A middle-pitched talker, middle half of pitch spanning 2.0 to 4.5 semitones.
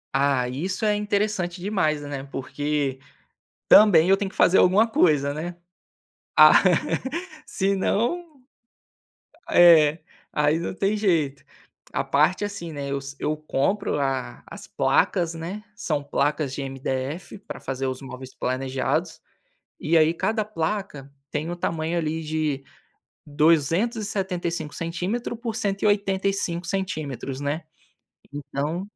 No: medium, 165 Hz; wide, 5.4 semitones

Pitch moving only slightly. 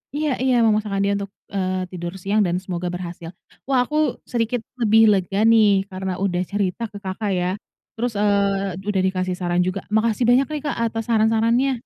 No: average, 3.5 semitones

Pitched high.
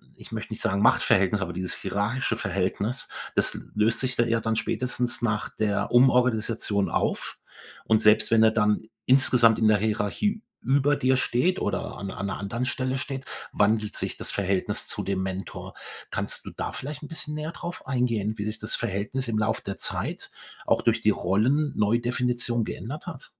No: low, 115 Hz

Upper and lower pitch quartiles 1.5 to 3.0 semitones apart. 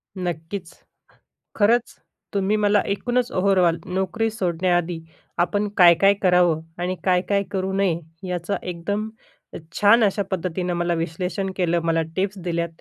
Yes: average, 2.7 semitones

